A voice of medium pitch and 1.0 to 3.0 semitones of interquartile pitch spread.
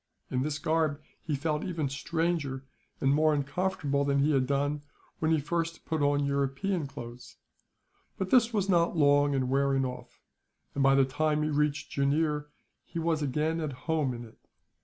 Yes: medium, 145 Hz; average, 2.7 semitones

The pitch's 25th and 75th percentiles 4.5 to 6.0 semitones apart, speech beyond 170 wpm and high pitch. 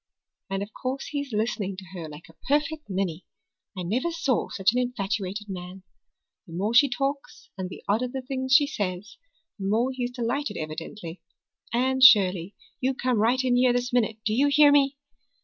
Yes: average, 5.2 semitones; average, 185 wpm; high, 235 Hz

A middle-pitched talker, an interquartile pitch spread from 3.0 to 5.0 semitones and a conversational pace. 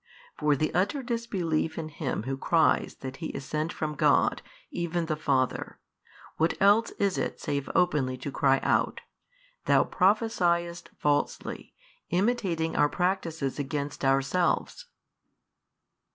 No: medium, 160 Hz; average, 4.2 semitones; slow, 125 wpm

